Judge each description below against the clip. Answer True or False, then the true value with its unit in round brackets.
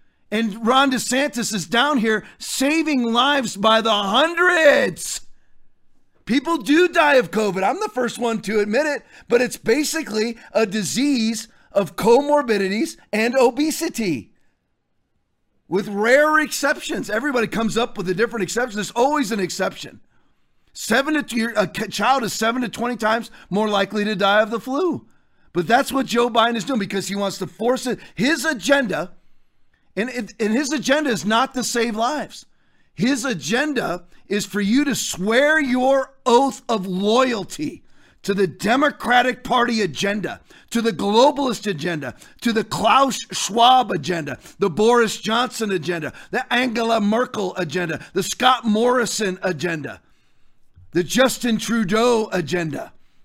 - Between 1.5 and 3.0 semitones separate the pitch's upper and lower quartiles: False (4.3 semitones)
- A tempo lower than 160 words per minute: True (145 wpm)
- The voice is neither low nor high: False (230 Hz)